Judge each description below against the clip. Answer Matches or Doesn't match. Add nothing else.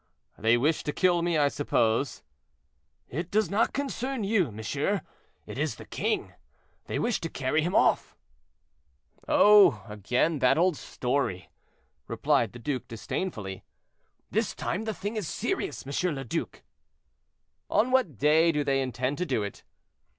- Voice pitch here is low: Doesn't match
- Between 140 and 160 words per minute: Matches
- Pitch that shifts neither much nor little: Doesn't match